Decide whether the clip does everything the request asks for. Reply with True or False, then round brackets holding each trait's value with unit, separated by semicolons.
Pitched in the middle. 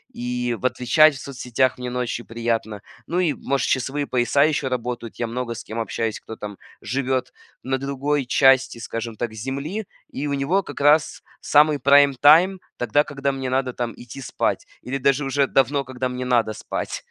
False (130 Hz)